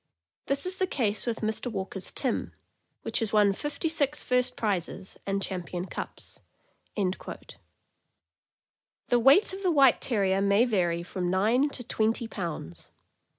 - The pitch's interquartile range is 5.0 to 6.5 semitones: Yes, average, 5.3 semitones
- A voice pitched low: No, high, 220 Hz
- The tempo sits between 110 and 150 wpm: Yes, average, 140 wpm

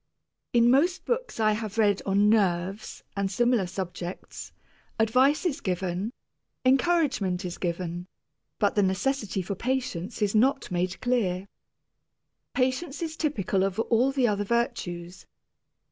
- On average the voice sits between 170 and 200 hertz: No, high, 210 Hz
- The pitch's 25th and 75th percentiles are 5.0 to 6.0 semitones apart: Yes, wide, 5.5 semitones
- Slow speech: Yes, slow, 130 wpm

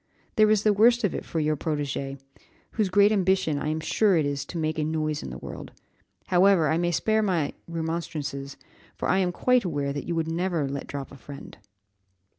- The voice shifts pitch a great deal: No, average, 4.6 semitones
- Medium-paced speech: No, fast, 210 wpm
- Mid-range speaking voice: Yes, medium, 160 Hz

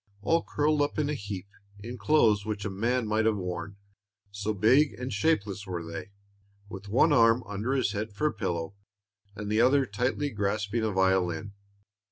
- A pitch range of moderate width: Yes, average, 3.9 semitones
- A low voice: Yes, low, 105 Hz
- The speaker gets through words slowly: No, average, 180 wpm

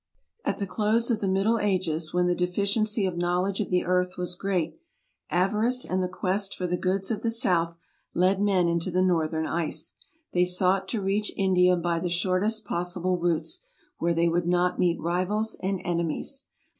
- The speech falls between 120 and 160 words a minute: No, average, 180 wpm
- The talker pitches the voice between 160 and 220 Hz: Yes, medium, 185 Hz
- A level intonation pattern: Yes, narrow, 2.2 semitones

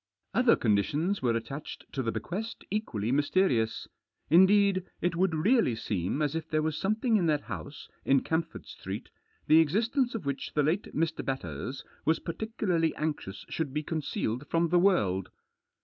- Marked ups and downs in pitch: Yes, wide, 5.8 semitones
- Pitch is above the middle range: No, medium, 160 Hz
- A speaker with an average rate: Yes, average, 165 wpm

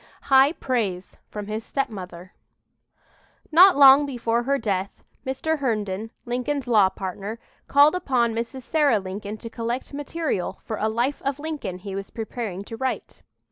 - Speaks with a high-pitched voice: Yes, high, 235 Hz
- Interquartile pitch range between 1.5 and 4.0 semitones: No, average, 5.2 semitones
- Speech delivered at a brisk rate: No, average, 145 wpm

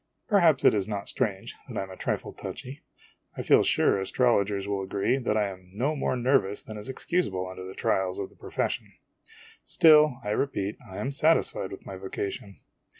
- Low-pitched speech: Yes, low, 105 Hz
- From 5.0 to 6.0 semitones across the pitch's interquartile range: Yes, wide, 5.5 semitones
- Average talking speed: Yes, average, 190 wpm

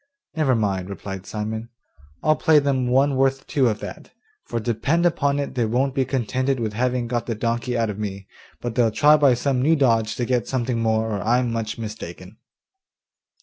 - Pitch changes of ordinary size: Yes, average, 3.4 semitones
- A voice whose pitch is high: No, low, 120 Hz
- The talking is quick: No, average, 190 wpm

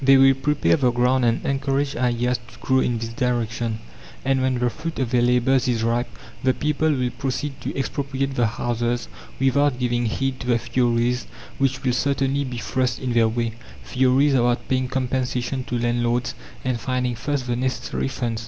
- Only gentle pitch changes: Yes, narrow, 1.9 semitones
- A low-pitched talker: Yes, low, 125 Hz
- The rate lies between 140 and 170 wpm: No, average, 180 wpm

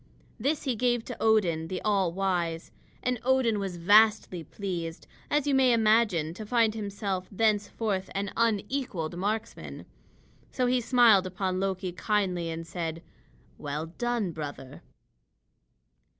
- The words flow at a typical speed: No, slow, 130 wpm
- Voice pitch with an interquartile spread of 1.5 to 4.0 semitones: No, average, 4.5 semitones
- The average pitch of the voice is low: No, high, 200 Hz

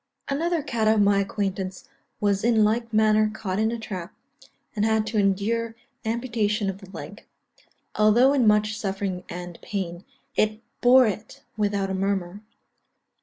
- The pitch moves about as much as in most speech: No, narrow, 2.3 semitones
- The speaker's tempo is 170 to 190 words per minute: No, average, 155 wpm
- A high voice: Yes, high, 210 Hz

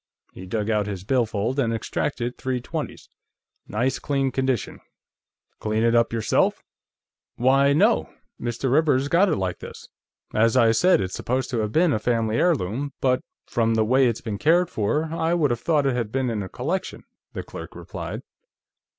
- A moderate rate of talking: Yes, average, 175 wpm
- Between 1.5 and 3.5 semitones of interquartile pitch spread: No, average, 4.0 semitones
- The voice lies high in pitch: No, low, 125 Hz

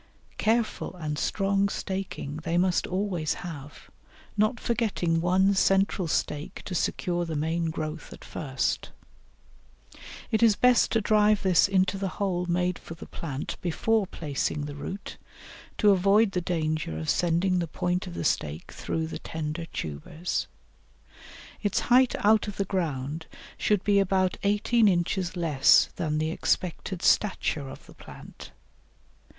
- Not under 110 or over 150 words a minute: Yes, average, 145 wpm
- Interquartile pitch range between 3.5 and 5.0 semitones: Yes, average, 3.8 semitones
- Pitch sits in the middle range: Yes, medium, 180 Hz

